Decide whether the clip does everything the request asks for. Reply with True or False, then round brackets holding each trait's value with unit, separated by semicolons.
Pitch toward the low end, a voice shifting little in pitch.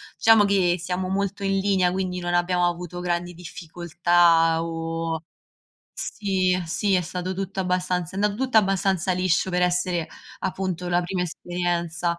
False (180 Hz; 1.7 semitones)